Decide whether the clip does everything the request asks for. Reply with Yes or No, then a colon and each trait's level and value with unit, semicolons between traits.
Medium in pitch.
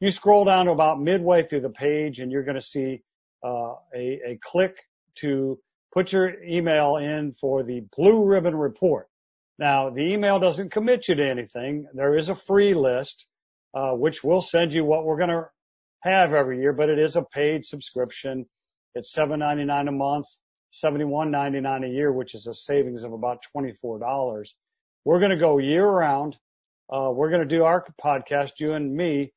Yes: medium, 145 Hz